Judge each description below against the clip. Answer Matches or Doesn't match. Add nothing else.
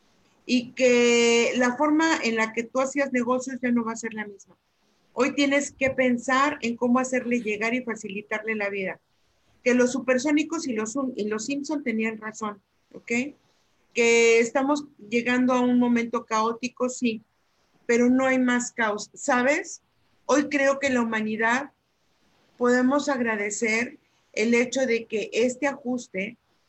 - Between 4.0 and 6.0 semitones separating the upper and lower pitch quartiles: Doesn't match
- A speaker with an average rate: Matches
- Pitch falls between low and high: Doesn't match